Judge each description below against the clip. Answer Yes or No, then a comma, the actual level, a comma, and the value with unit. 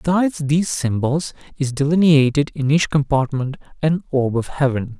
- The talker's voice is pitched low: No, medium, 145 Hz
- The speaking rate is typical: Yes, average, 145 wpm